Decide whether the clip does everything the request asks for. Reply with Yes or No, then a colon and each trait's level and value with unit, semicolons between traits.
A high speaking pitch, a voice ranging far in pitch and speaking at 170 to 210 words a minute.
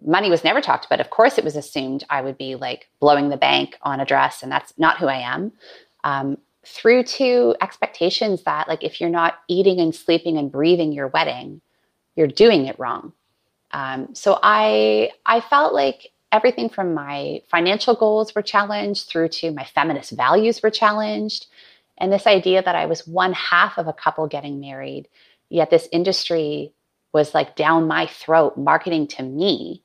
No: medium, 165 Hz; wide, 5.8 semitones; average, 180 wpm